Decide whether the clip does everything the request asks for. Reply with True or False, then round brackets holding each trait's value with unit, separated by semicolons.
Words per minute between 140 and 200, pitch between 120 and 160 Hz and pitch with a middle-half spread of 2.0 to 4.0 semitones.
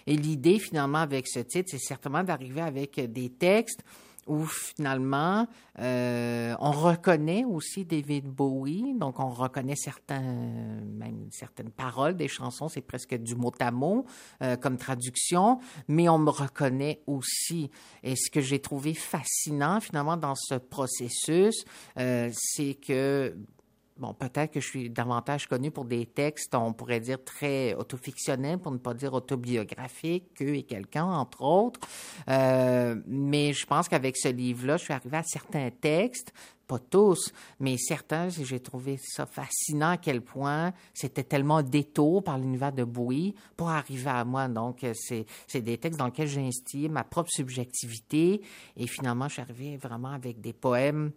True (160 wpm; 140 Hz; 3.6 semitones)